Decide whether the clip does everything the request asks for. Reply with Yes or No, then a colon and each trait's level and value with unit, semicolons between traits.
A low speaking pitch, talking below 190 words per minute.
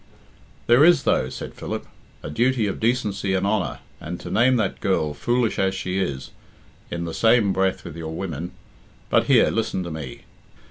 Yes: very low, 95 Hz; average, 180 wpm